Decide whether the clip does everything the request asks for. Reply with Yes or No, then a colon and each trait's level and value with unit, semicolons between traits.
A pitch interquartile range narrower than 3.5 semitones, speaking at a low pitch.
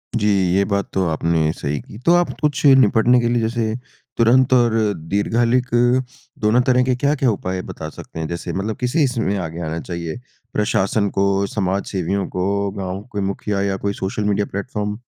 No: average, 3.8 semitones; low, 100 Hz